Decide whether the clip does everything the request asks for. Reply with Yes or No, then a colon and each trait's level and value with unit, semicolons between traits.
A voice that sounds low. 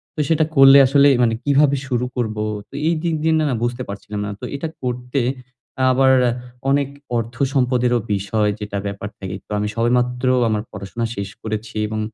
Yes: low, 125 Hz